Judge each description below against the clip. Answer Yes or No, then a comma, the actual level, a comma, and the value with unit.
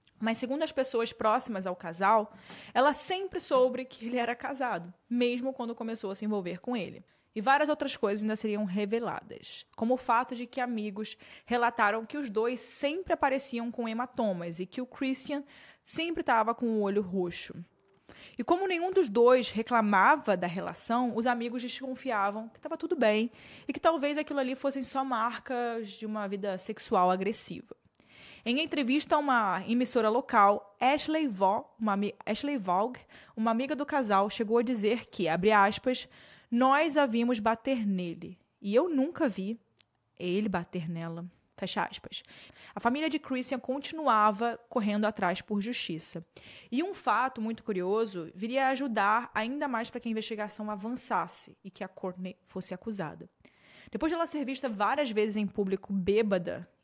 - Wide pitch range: No, average, 4.3 semitones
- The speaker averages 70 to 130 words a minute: No, average, 165 wpm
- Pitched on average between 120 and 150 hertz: No, high, 230 Hz